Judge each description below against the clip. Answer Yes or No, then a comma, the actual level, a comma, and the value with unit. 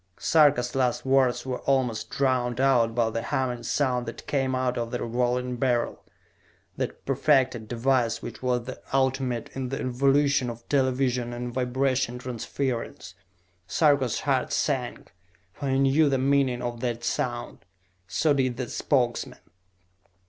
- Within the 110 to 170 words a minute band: Yes, average, 140 wpm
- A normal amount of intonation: No, narrow, 1.9 semitones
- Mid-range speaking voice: No, low, 125 Hz